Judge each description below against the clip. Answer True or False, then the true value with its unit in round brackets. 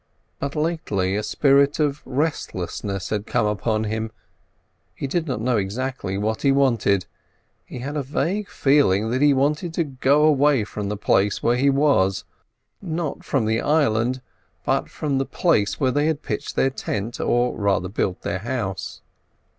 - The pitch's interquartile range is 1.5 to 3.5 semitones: False (5.5 semitones)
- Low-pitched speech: True (130 Hz)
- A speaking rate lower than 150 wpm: False (165 wpm)